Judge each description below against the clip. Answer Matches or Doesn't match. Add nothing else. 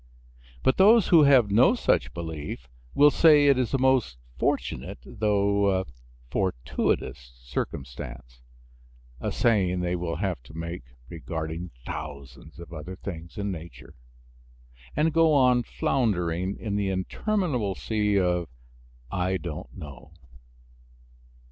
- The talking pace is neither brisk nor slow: Doesn't match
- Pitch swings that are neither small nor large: Doesn't match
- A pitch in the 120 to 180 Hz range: Doesn't match